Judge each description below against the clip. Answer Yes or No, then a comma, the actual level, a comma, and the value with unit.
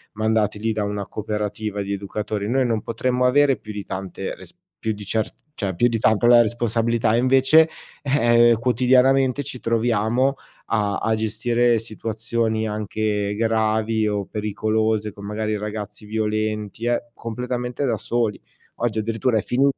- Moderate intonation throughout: No, narrow, 2.1 semitones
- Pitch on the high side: No, low, 110 Hz